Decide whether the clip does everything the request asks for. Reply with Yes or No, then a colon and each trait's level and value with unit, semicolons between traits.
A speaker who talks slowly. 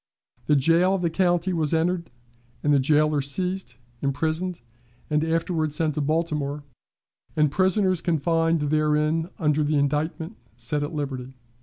Yes: slow, 130 wpm